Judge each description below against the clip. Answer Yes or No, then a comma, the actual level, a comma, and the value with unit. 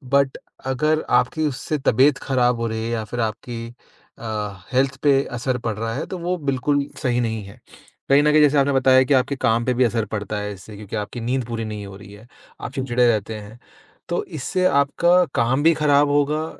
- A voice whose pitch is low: Yes, low, 125 Hz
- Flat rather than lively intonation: No, average, 4.2 semitones